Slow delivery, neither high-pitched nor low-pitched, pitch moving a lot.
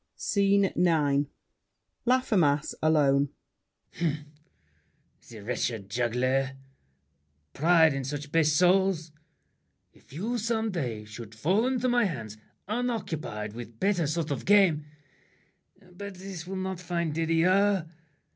Yes: slow, 110 wpm; medium, 165 Hz; wide, 5.9 semitones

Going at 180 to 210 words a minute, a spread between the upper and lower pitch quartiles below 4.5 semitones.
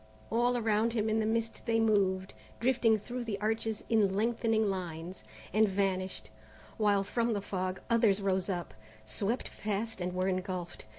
No: average, 160 wpm; average, 3.0 semitones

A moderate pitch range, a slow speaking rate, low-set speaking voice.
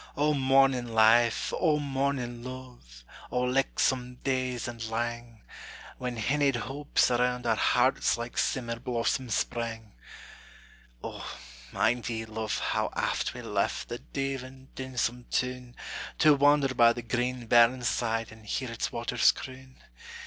No: narrow, 2.0 semitones; slow, 130 wpm; low, 125 Hz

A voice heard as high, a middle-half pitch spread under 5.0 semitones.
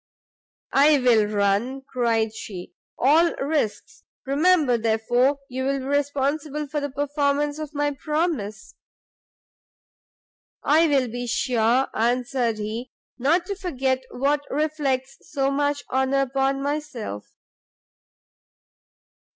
Yes: very high, 275 Hz; average, 3.1 semitones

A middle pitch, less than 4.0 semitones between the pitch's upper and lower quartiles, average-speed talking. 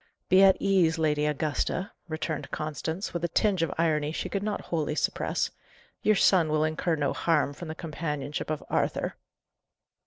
Yes: medium, 160 Hz; narrow, 2.6 semitones; average, 165 wpm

